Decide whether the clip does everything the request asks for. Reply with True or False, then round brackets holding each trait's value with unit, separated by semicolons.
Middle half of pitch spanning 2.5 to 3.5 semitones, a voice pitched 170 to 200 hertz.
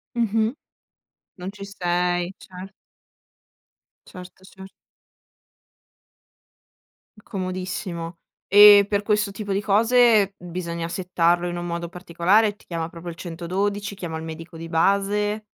True (2.9 semitones; 185 Hz)